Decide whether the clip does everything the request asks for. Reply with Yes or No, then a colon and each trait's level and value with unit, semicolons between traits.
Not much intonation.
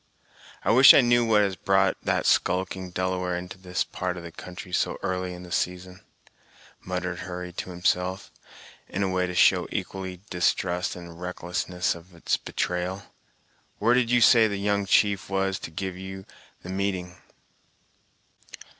Yes: narrow, 1.4 semitones